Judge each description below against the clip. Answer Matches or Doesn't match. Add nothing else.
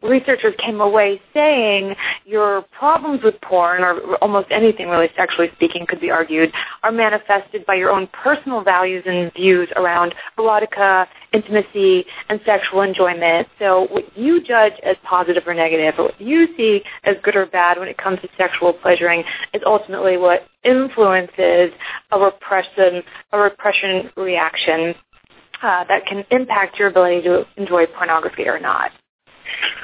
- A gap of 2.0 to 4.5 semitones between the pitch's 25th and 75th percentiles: Matches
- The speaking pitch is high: Matches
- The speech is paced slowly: Doesn't match